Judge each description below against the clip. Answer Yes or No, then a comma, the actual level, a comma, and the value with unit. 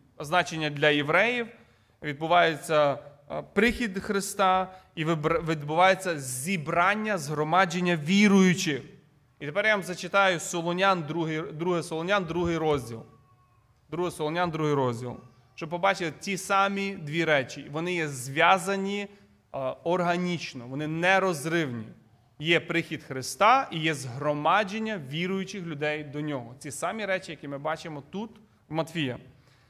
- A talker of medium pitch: Yes, medium, 165 Hz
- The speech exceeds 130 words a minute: No, average, 115 wpm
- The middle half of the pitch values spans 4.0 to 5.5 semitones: Yes, average, 4.3 semitones